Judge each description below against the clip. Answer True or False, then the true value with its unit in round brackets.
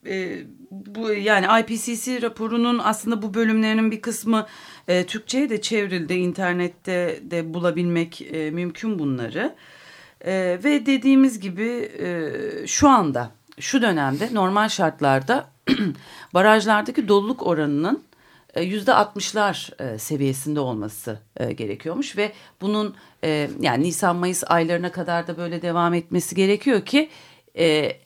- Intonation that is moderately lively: True (4.8 semitones)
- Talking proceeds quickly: False (120 wpm)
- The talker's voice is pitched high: True (195 Hz)